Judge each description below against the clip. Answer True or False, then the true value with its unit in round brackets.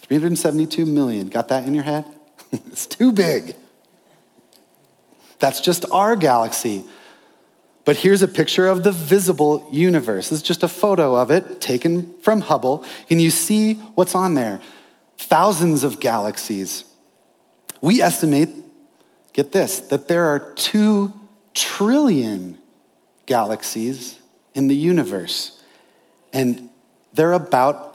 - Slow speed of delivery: True (120 wpm)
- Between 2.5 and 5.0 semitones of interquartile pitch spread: False (5.6 semitones)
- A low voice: False (160 Hz)